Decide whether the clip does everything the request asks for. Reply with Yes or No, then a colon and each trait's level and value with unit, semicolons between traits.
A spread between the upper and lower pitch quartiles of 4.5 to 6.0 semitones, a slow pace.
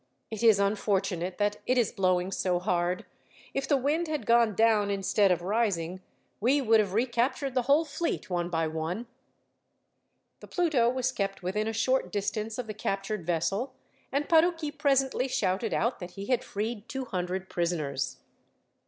No: wide, 5.4 semitones; average, 165 wpm